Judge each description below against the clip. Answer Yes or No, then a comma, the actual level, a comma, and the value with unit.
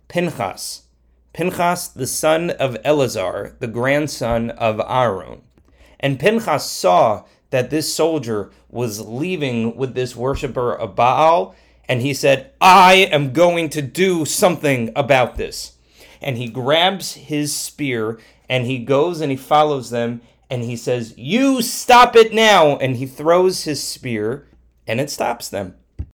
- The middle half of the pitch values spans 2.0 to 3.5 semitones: No, wide, 5.5 semitones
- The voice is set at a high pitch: No, medium, 140 Hz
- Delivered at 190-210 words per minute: No, average, 140 wpm